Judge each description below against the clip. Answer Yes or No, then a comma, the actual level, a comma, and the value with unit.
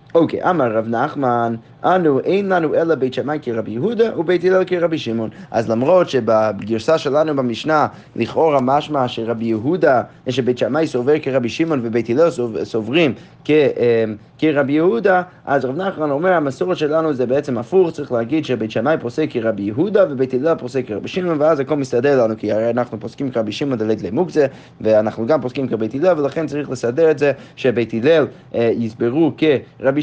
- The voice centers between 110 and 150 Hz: Yes, low, 135 Hz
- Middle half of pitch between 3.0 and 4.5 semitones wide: No, average, 5.2 semitones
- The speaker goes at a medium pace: No, fast, 170 wpm